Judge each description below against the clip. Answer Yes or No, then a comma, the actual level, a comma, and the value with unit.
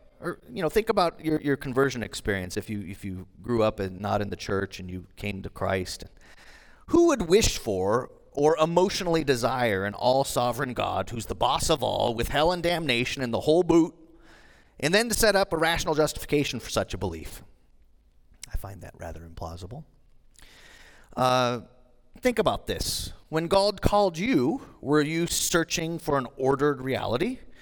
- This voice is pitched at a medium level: No, low, 125 Hz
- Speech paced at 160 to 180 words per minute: Yes, average, 175 wpm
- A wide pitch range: Yes, wide, 8.5 semitones